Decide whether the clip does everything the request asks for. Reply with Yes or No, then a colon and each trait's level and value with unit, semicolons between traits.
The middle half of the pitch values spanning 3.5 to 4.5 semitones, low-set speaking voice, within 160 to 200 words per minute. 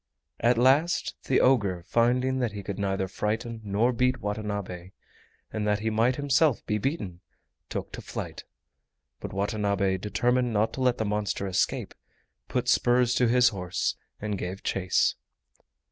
No: average, 3.8 semitones; low, 110 Hz; average, 150 wpm